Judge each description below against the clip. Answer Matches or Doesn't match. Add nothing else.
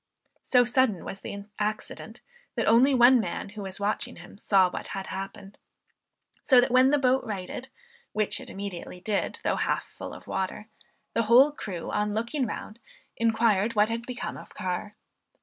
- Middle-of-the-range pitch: Doesn't match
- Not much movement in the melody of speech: Doesn't match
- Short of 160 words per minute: Doesn't match